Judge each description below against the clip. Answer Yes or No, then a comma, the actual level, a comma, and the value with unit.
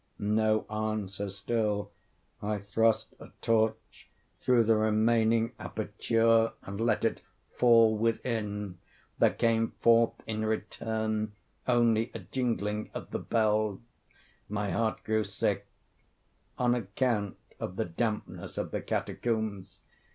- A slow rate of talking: Yes, slow, 115 wpm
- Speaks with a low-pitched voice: Yes, low, 110 Hz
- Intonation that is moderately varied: No, narrow, 1.6 semitones